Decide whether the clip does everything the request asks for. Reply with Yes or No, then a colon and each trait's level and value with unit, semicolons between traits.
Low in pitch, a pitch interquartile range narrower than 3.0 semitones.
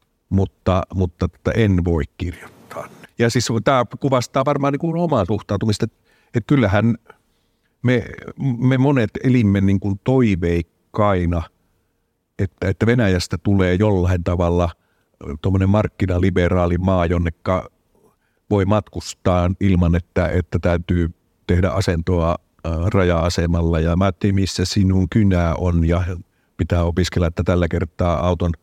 No: very low, 95 Hz; average, 3.5 semitones